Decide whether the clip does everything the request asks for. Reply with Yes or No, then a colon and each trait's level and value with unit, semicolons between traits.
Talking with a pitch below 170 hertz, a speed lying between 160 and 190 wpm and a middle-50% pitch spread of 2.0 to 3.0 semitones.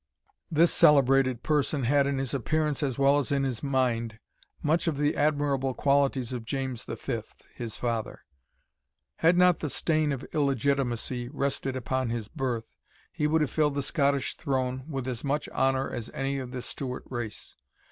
Yes: low, 135 Hz; average, 165 wpm; narrow, 2.4 semitones